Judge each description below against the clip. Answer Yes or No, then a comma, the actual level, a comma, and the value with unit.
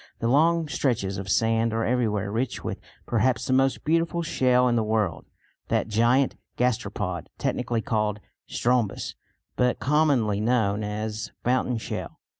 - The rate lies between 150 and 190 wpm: No, average, 140 wpm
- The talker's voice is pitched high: No, low, 115 Hz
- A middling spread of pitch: Yes, average, 3.2 semitones